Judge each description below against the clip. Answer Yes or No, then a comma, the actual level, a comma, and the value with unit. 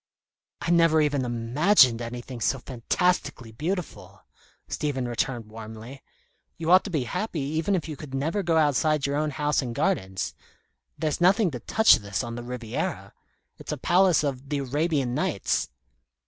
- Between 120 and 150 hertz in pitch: Yes, medium, 140 Hz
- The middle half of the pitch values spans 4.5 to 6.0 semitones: Yes, average, 5.2 semitones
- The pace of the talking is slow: No, average, 160 wpm